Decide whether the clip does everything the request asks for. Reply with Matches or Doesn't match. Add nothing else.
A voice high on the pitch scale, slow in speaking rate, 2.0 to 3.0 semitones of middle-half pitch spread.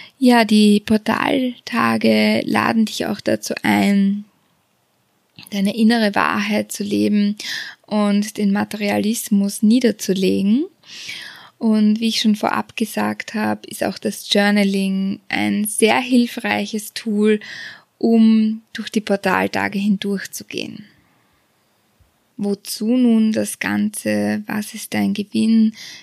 Matches